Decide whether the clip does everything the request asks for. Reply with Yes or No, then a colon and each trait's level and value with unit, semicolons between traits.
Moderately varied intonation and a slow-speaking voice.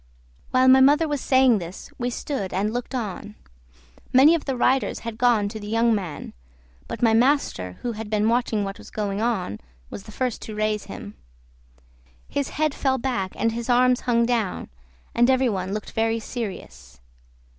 No: average, 3.5 semitones; average, 180 wpm